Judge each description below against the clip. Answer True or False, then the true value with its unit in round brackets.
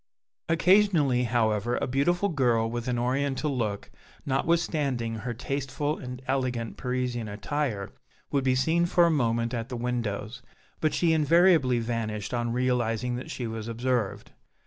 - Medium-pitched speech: False (125 Hz)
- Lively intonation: False (3.5 semitones)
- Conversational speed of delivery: True (145 wpm)